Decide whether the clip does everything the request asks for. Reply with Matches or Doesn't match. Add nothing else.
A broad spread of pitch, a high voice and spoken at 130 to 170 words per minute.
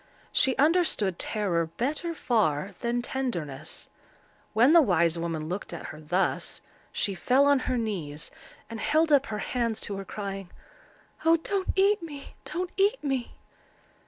Matches